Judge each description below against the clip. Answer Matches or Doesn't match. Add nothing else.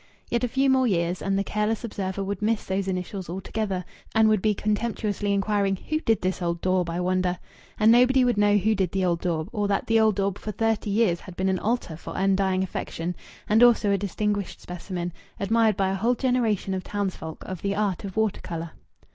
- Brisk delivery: Matches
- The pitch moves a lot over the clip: Doesn't match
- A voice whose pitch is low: Doesn't match